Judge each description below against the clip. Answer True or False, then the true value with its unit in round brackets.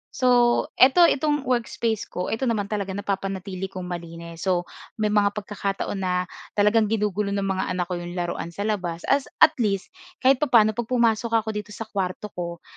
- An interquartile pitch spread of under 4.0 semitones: True (3.5 semitones)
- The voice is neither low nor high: False (205 Hz)